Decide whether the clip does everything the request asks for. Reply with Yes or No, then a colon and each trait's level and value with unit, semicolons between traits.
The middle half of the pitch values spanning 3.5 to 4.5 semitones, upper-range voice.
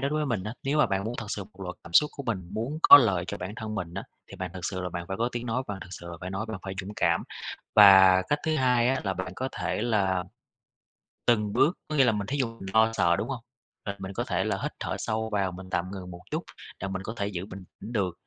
No: average, 4.1 semitones; low, 100 Hz